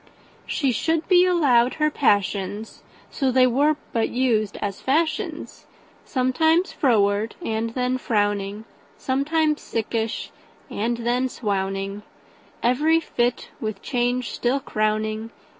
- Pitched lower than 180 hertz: No, high, 240 Hz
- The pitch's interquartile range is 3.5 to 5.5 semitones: Yes, average, 4.4 semitones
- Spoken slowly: Yes, slow, 95 wpm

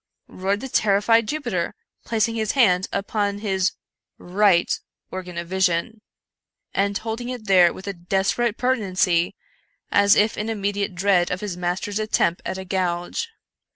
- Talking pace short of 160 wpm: Yes, average, 150 wpm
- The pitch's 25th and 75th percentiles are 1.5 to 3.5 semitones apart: Yes, average, 3.0 semitones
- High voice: Yes, high, 200 Hz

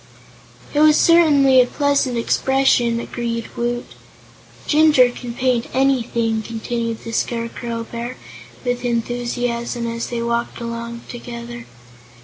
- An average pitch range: No, narrow, 1.6 semitones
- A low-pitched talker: No, high, 240 Hz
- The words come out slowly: Yes, slow, 115 wpm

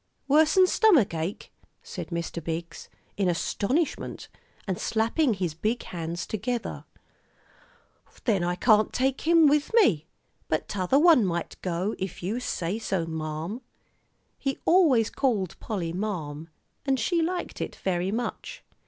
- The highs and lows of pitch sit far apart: Yes, wide, 7.8 semitones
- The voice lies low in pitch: No, high, 210 Hz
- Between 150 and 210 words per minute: No, slow, 135 wpm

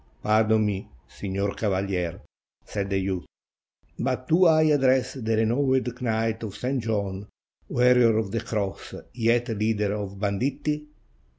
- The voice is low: Yes, low, 110 Hz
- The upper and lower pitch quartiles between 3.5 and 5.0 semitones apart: Yes, average, 3.8 semitones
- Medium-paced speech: No, slow, 130 wpm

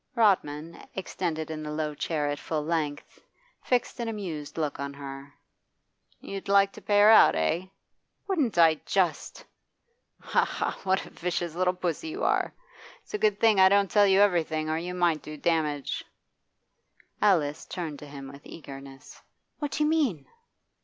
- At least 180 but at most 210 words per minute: No, average, 165 wpm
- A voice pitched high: No, medium, 170 Hz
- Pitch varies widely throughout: No, average, 4.9 semitones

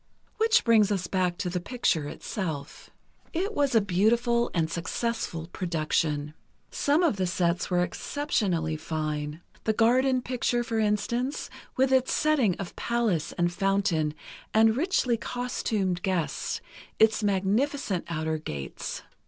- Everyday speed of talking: No, slow, 130 wpm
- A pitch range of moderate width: No, wide, 6.0 semitones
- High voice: Yes, high, 200 Hz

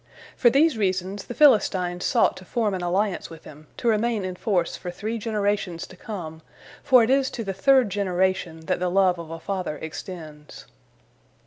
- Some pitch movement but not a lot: Yes, average, 3.8 semitones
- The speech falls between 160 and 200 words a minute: Yes, average, 185 wpm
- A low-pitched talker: No, high, 190 Hz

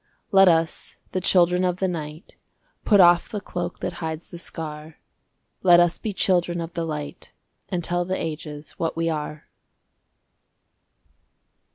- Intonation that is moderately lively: No, narrow, 1.9 semitones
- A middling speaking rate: Yes, average, 150 wpm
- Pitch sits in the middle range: Yes, medium, 175 Hz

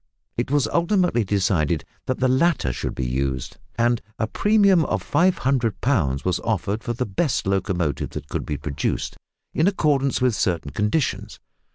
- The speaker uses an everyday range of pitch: No, wide, 8.3 semitones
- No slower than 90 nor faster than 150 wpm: No, average, 160 wpm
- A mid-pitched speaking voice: No, low, 115 Hz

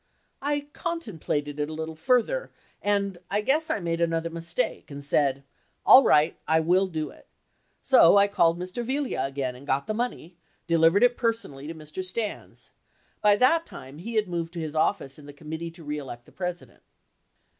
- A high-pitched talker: No, medium, 170 Hz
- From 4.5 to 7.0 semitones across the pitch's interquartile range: Yes, wide, 5.6 semitones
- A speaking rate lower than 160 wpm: No, average, 185 wpm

